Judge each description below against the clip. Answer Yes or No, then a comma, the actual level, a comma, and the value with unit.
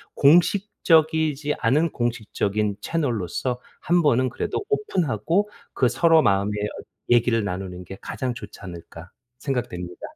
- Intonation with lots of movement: Yes, wide, 7.6 semitones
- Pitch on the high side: No, low, 125 Hz